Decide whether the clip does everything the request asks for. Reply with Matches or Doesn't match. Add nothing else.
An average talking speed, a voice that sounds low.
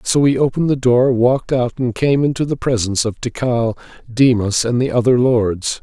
Matches